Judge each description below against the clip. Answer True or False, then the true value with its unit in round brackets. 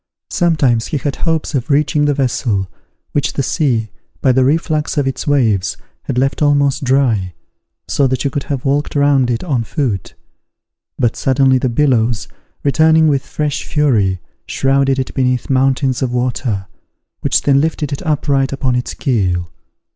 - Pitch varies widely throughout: False (2.8 semitones)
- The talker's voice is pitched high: False (135 Hz)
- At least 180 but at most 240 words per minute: False (160 wpm)